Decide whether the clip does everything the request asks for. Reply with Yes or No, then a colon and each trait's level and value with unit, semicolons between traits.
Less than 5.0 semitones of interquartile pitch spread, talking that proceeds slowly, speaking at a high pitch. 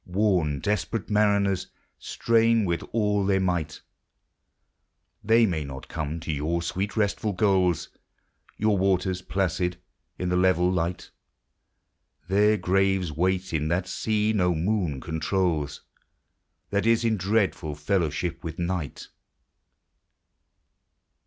No: average, 3.5 semitones; slow, 120 wpm; very low, 90 Hz